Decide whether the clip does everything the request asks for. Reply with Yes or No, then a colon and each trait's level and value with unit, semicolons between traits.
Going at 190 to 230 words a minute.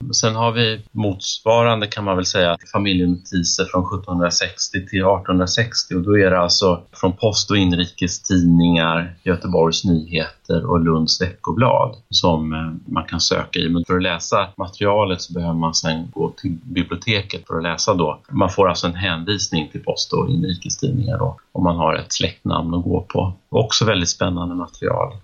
No: average, 165 wpm